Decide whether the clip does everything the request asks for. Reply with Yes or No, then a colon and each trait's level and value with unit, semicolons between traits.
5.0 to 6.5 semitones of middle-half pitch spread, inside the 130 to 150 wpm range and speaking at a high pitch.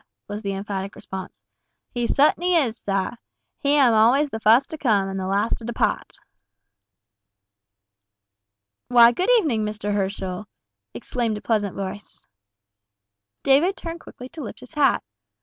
Yes: average, 5.3 semitones; average, 140 wpm; high, 225 Hz